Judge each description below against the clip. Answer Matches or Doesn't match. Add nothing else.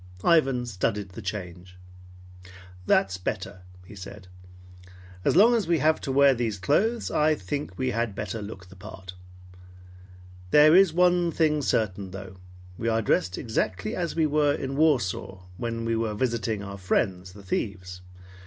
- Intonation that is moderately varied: Doesn't match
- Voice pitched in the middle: Doesn't match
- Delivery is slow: Doesn't match